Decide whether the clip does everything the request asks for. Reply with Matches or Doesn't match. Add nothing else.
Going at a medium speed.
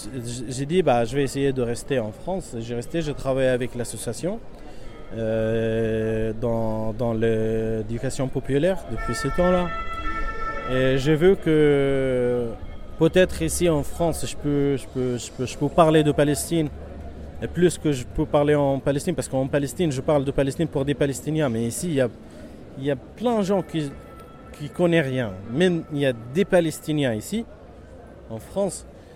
Matches